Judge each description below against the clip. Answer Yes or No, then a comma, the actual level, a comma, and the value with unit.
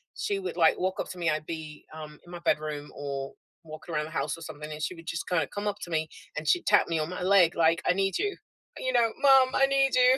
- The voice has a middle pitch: Yes, medium, 170 Hz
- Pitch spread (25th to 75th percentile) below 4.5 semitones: No, average, 4.8 semitones